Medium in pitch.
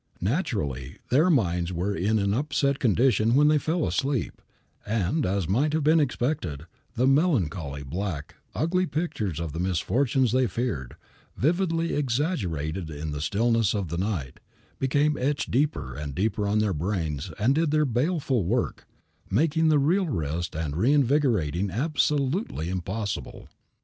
No: low, 115 Hz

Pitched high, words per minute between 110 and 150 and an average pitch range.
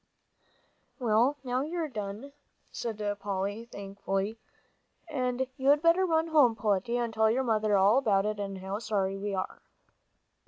Yes: high, 220 Hz; average, 145 wpm; average, 4.6 semitones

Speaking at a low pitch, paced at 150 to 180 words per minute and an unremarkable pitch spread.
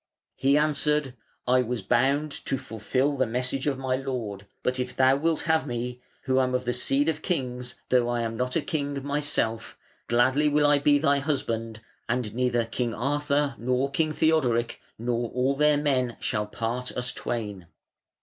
Yes: low, 130 Hz; average, 175 wpm; average, 3.0 semitones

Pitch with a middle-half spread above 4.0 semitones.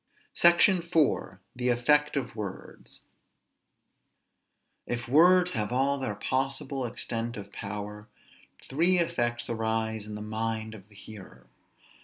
Yes: average, 4.5 semitones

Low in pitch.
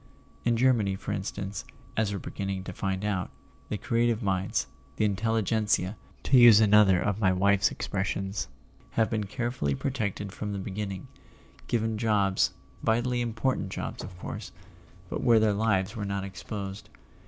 Yes: low, 105 Hz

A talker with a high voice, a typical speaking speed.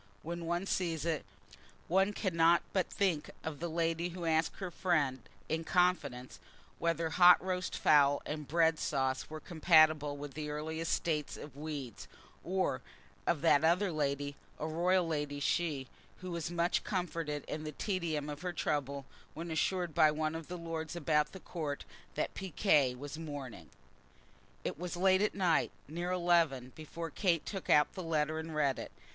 No: medium, 160 Hz; average, 165 wpm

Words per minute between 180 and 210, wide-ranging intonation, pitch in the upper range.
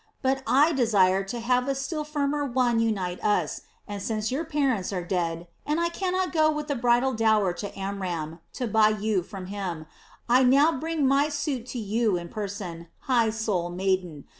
Yes: average, 185 wpm; wide, 6.1 semitones; high, 225 Hz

